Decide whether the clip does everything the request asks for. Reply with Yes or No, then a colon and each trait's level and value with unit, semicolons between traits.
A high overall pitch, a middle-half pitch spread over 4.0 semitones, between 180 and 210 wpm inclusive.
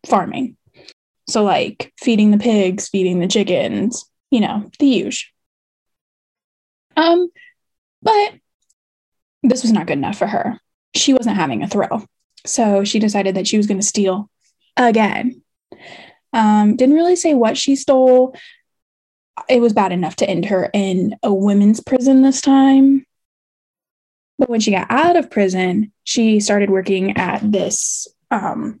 No: high, 225 Hz; average, 5.1 semitones; average, 145 wpm